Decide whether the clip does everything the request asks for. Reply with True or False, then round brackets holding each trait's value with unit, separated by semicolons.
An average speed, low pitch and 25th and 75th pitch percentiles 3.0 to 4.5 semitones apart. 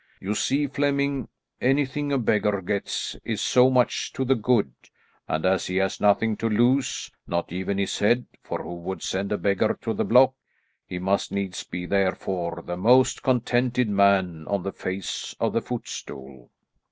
False (170 wpm; 100 Hz; 5.2 semitones)